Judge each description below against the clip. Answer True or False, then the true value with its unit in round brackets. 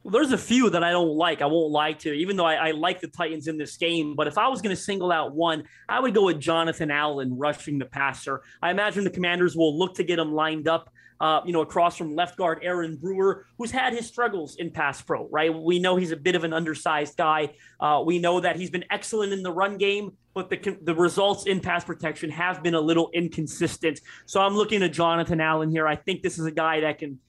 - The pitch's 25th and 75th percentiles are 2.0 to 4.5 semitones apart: True (2.7 semitones)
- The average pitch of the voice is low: False (170 Hz)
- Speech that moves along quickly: True (255 wpm)